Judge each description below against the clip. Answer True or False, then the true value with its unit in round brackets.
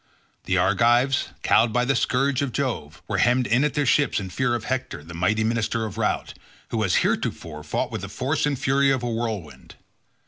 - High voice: False (120 Hz)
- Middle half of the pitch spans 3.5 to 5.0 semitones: True (4.1 semitones)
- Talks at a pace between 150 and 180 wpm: False (205 wpm)